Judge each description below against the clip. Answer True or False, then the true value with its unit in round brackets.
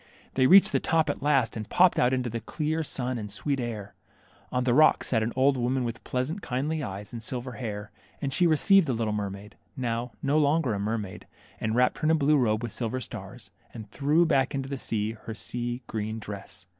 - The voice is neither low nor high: False (125 Hz)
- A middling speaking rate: False (220 wpm)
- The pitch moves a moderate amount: True (4.3 semitones)